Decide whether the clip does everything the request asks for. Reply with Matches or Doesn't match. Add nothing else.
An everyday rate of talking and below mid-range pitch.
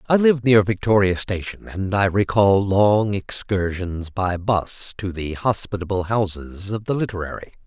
Matches